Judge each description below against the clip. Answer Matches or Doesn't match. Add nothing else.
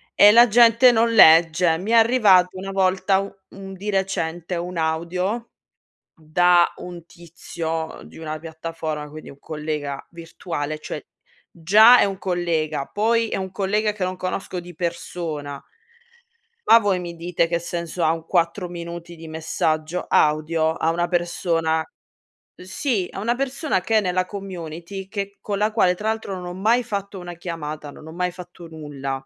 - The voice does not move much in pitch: Doesn't match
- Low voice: Doesn't match